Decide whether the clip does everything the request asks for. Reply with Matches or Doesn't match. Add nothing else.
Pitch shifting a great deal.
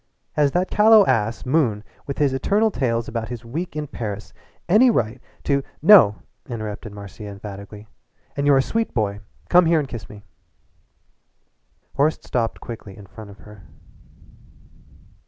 Matches